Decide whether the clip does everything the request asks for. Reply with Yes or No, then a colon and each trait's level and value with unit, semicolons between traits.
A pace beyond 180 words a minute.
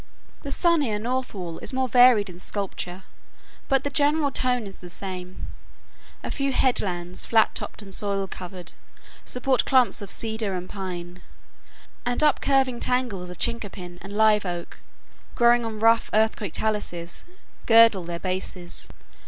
No: average, 145 wpm